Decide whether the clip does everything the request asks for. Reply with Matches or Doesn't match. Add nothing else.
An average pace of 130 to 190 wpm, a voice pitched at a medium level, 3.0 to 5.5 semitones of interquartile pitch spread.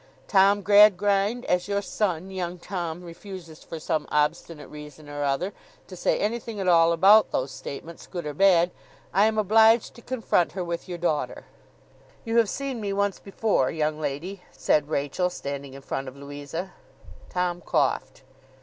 Matches